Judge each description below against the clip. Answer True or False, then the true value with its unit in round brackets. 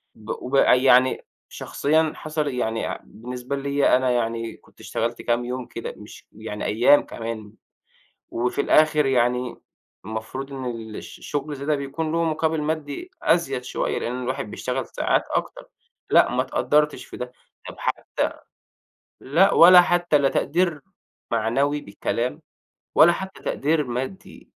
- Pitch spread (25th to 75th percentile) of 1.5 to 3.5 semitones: False (4.1 semitones)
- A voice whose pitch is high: False (135 Hz)